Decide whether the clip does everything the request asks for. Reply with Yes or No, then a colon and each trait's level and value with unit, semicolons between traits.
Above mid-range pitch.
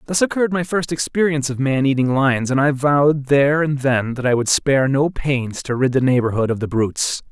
No: medium, 140 Hz